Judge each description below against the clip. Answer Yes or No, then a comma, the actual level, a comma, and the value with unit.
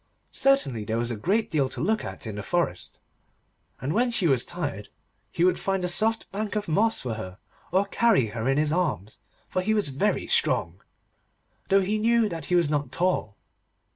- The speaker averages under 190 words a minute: No, average, 200 wpm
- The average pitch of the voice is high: No, medium, 175 Hz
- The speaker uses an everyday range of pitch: No, wide, 8.3 semitones